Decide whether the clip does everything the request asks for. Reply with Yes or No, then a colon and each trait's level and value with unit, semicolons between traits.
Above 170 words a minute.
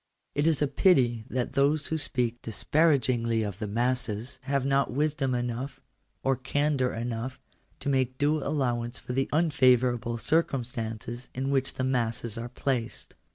No: average, 160 wpm